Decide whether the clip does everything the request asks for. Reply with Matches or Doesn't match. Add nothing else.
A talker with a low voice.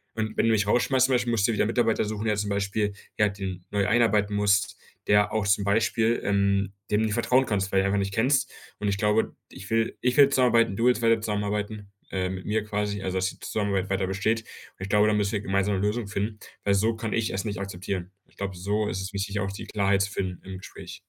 Matches